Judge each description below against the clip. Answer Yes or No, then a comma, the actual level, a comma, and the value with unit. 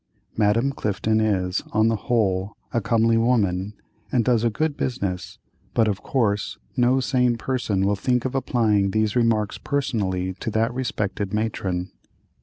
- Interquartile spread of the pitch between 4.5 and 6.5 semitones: No, average, 3.4 semitones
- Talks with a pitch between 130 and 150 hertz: No, low, 110 Hz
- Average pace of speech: Yes, average, 150 wpm